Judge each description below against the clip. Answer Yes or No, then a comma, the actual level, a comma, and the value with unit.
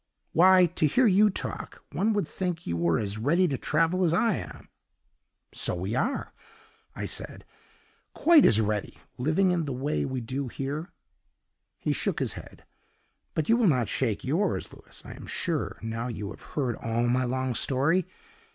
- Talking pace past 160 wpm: Yes, average, 175 wpm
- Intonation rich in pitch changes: Yes, wide, 7.2 semitones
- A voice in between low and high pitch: Yes, medium, 145 Hz